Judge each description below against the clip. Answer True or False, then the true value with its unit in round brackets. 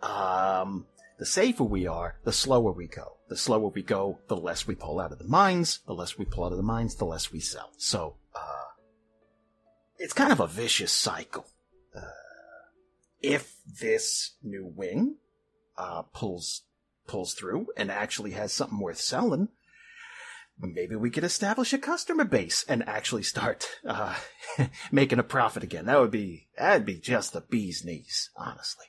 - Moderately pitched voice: True (170 Hz)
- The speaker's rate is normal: True (170 wpm)